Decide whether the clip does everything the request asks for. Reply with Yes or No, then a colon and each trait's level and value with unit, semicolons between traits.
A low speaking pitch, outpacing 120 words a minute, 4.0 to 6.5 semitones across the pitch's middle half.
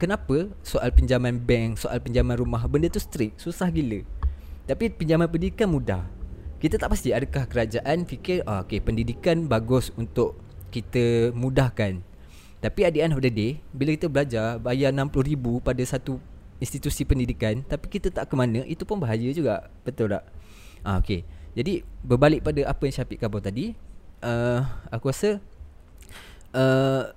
Yes: low, 125 Hz; average, 150 wpm; average, 5.3 semitones